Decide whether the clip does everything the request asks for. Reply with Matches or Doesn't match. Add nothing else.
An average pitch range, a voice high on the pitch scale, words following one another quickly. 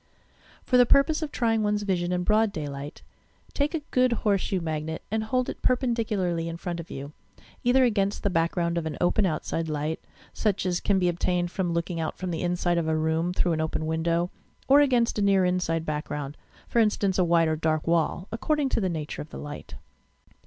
Doesn't match